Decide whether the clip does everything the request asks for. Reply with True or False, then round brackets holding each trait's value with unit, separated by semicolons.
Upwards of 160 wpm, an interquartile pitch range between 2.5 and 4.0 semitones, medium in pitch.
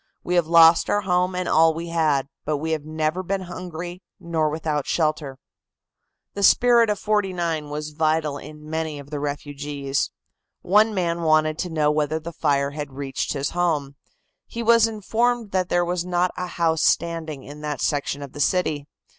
True (180 wpm; 3.3 semitones; 160 Hz)